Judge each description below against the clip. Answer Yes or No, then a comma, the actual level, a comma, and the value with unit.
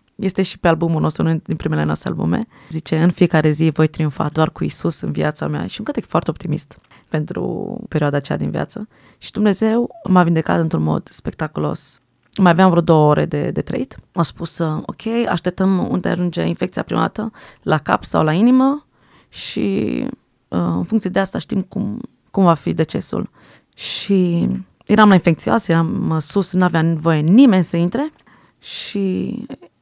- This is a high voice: No, medium, 170 Hz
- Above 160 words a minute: Yes, fast, 170 wpm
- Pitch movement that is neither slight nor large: Yes, average, 4.1 semitones